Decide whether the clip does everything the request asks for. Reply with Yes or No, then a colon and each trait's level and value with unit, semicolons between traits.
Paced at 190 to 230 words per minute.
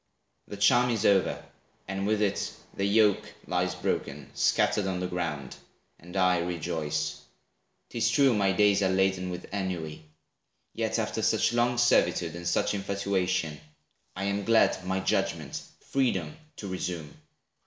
No: average, 145 wpm